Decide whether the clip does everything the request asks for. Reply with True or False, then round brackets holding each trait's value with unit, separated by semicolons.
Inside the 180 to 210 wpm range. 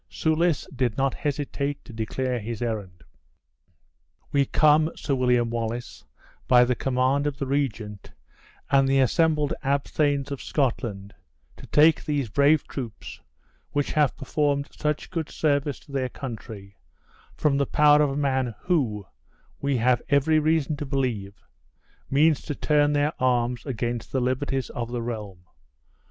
False (145 wpm)